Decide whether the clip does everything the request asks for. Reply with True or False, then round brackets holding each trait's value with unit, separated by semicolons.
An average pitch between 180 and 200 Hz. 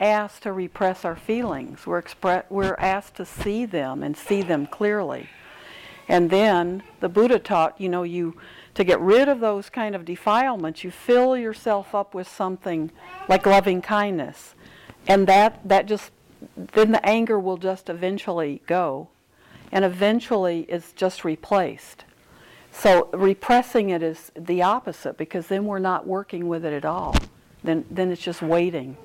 True (190 Hz)